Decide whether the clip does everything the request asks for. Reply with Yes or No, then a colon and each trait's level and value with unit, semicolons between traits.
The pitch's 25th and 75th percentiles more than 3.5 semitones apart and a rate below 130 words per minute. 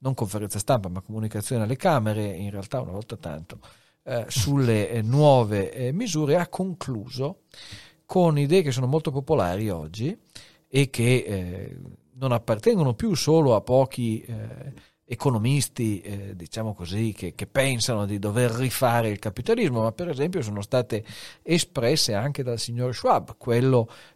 No: average, 4.4 semitones; average, 150 wpm